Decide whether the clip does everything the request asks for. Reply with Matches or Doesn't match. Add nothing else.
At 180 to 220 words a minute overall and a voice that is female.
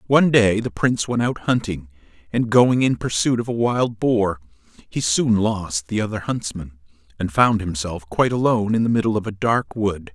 Doesn't match